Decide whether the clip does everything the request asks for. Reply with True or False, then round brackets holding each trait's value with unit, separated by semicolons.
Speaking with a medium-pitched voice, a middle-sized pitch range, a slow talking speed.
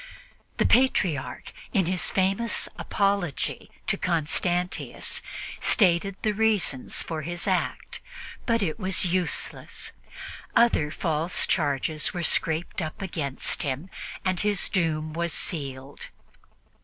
True (175 Hz; 3.8 semitones; 110 wpm)